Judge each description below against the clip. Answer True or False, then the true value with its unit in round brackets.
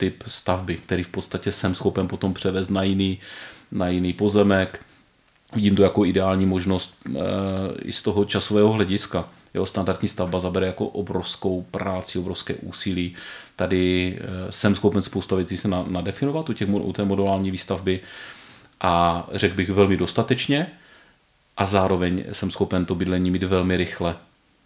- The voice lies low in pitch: True (95 Hz)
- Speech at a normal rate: True (145 wpm)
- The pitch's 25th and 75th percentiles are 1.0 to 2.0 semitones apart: True (1.7 semitones)